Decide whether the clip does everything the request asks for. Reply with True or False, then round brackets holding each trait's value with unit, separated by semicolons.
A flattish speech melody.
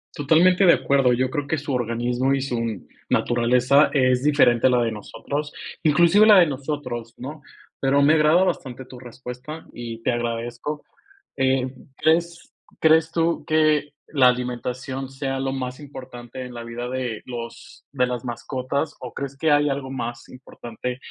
False (3.2 semitones)